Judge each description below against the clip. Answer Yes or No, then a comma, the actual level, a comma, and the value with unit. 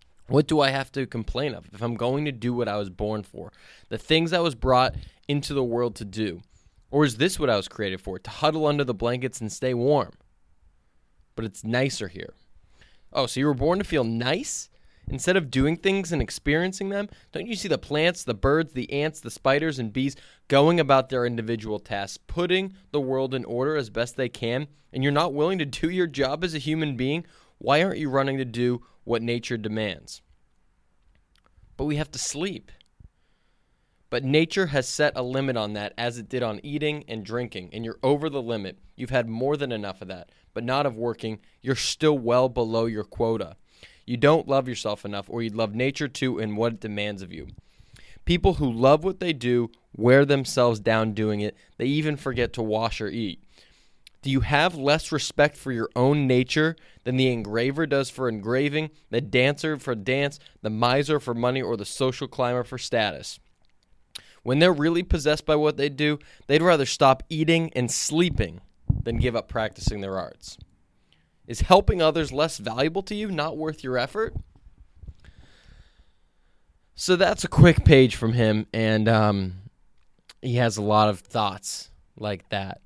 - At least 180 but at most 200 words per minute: Yes, average, 190 wpm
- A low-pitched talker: Yes, low, 125 Hz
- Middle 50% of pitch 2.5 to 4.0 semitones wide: No, average, 5.2 semitones